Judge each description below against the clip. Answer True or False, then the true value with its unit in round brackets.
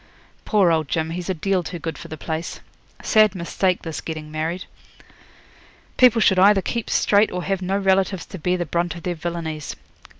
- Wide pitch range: False (3.1 semitones)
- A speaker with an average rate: True (190 wpm)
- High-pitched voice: False (180 Hz)